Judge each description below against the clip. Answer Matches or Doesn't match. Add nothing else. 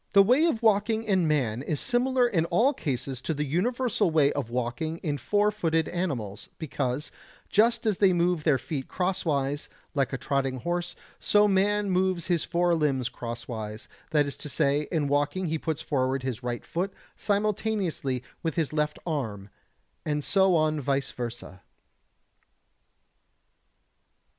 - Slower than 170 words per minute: Matches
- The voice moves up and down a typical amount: Doesn't match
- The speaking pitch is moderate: Matches